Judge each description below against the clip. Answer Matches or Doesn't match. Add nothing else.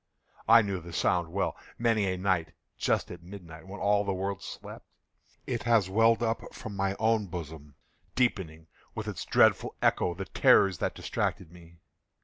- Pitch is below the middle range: Matches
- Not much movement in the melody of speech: Doesn't match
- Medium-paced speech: Matches